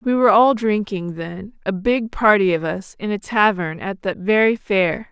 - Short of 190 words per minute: No, average, 200 wpm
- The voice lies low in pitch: No, high, 205 Hz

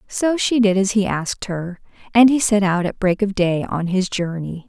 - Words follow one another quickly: Yes, fast, 230 wpm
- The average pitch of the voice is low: No, high, 195 Hz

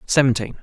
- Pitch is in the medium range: No, low, 130 Hz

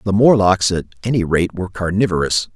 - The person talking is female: No, male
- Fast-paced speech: No, average, 165 wpm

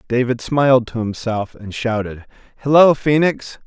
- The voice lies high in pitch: No, low, 120 Hz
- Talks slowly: Yes, slow, 130 wpm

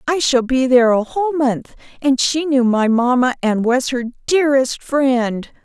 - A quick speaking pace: No, average, 180 wpm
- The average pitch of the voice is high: Yes, very high, 260 Hz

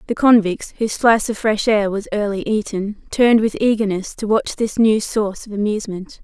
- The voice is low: No, high, 215 Hz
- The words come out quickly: No, average, 175 wpm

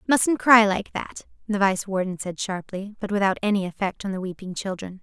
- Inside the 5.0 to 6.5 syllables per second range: Yes, 5.2 syllables/s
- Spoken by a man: No, female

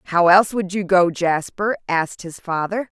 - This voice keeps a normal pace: Yes, average, 180 wpm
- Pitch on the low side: No, medium, 185 Hz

